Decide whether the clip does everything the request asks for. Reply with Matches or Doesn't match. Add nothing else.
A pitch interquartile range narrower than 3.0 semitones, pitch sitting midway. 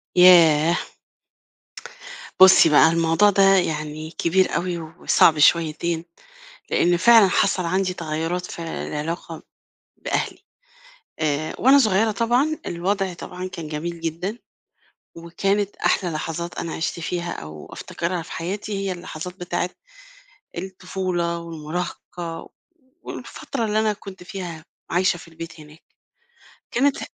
Matches